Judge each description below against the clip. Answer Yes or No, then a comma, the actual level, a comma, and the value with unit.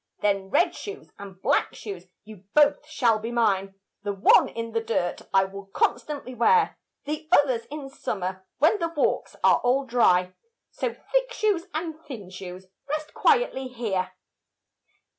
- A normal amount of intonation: No, wide, 7.6 semitones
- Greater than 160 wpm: No, average, 155 wpm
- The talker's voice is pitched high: Yes, high, 235 Hz